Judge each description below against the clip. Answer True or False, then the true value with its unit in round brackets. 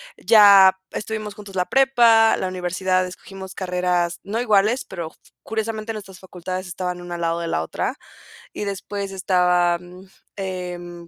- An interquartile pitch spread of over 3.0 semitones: False (2.6 semitones)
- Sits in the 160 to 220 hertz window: True (185 Hz)